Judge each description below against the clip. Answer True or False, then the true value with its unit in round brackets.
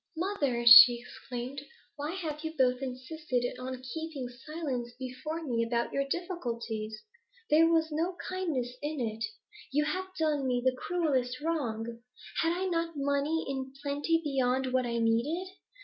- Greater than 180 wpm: False (150 wpm)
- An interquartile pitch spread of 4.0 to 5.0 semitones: True (4.5 semitones)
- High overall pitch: True (275 Hz)